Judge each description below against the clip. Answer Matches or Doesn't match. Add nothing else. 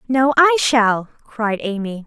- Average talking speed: Matches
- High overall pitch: Matches